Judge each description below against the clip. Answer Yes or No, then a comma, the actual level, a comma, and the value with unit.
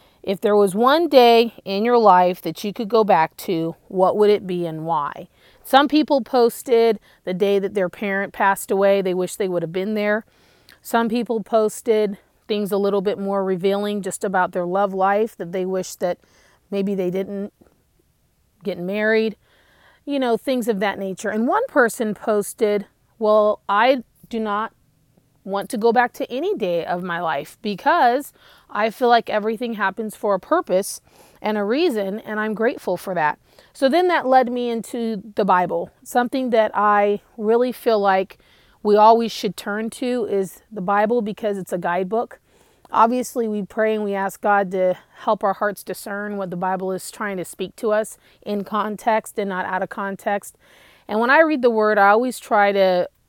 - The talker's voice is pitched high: Yes, high, 210 Hz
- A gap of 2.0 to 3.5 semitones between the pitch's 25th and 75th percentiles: Yes, average, 3.0 semitones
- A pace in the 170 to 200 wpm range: Yes, average, 185 wpm